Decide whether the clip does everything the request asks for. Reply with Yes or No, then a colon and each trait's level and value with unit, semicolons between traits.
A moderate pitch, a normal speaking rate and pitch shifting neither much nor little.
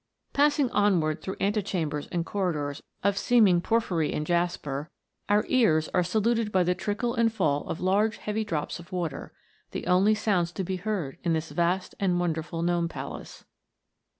Yes: medium, 180 Hz; average, 170 wpm; average, 3.9 semitones